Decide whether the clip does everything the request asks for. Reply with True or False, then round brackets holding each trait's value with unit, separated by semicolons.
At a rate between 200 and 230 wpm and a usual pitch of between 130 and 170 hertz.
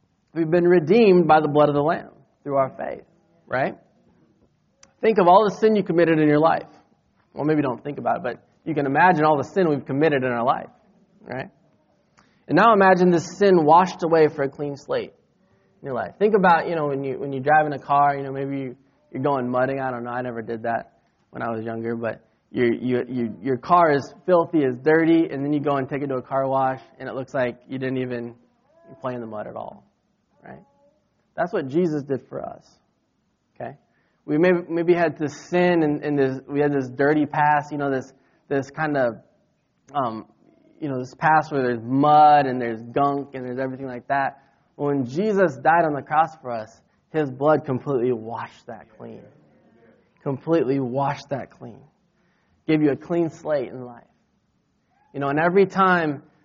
True (205 wpm; 140 Hz)